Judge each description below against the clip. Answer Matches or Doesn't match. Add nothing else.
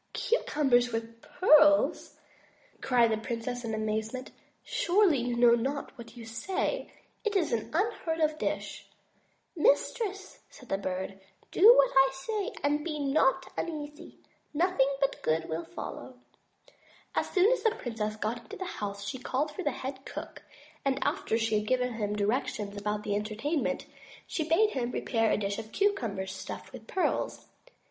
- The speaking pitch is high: Matches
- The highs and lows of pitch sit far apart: Matches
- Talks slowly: Doesn't match